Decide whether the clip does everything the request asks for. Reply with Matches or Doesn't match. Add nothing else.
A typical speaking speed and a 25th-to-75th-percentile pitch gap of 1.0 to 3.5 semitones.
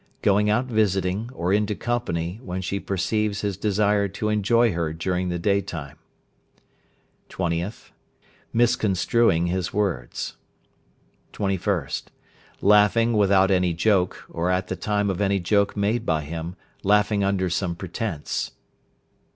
Doesn't match